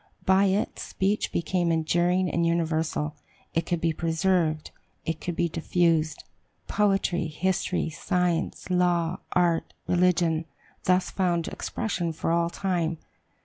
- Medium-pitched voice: Yes, medium, 170 Hz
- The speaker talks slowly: Yes, slow, 120 wpm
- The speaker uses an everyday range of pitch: No, narrow, 1.9 semitones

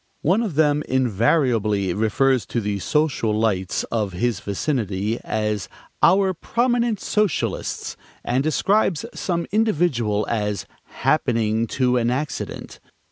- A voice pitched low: Yes, low, 125 Hz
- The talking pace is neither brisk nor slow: No, slow, 115 wpm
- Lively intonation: Yes, wide, 6.8 semitones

